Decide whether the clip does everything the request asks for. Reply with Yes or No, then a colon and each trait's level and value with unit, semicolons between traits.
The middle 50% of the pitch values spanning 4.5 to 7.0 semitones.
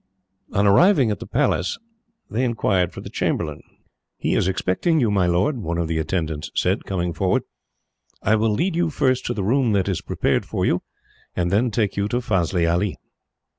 Yes: average, 5.3 semitones